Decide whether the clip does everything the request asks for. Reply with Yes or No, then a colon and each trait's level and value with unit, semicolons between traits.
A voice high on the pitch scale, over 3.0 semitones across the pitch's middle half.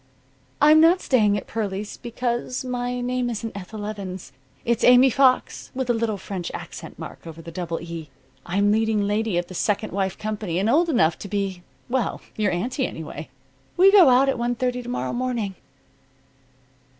Yes: high, 220 Hz; average, 4.4 semitones